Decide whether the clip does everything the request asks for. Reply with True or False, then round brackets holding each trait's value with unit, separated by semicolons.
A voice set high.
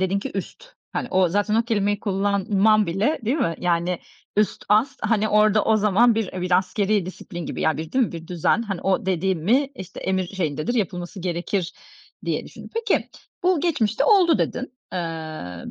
True (195 Hz)